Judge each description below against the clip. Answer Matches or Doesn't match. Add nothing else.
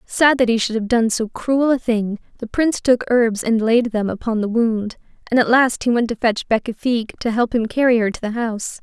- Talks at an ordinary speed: Doesn't match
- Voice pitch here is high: Matches